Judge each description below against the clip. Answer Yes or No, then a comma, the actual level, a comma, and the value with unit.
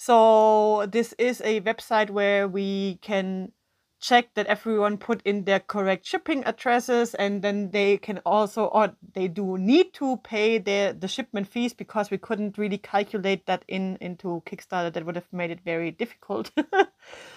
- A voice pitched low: No, high, 210 Hz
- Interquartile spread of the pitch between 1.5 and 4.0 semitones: Yes, average, 2.8 semitones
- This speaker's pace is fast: No, average, 165 wpm